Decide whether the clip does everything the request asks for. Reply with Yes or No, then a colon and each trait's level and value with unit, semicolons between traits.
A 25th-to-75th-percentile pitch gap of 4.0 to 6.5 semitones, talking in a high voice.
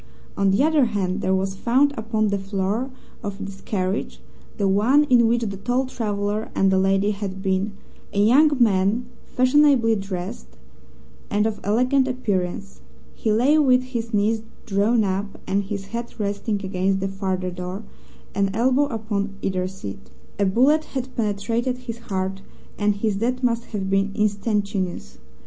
No: average, 3.4 semitones; high, 205 Hz